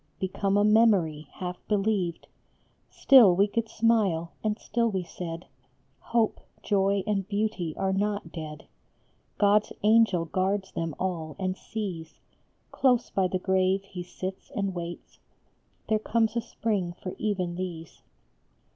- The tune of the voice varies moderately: Yes, average, 3.1 semitones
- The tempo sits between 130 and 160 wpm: Yes, average, 140 wpm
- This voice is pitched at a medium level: No, high, 195 Hz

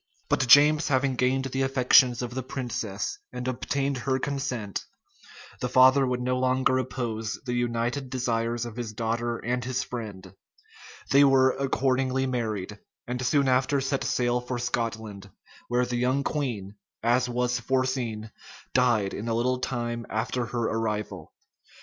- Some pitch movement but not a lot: No, narrow, 2.0 semitones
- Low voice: Yes, low, 125 Hz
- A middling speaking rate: Yes, average, 150 wpm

